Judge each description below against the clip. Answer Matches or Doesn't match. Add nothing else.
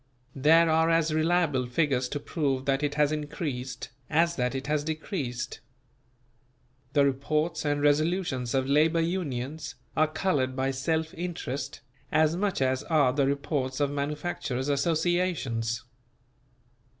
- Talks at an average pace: Doesn't match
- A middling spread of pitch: Matches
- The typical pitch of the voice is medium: Matches